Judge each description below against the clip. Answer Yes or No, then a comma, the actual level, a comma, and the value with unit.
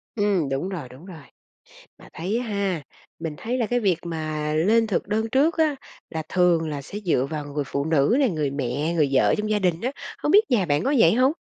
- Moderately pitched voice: Yes, medium, 175 Hz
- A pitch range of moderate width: No, wide, 6.5 semitones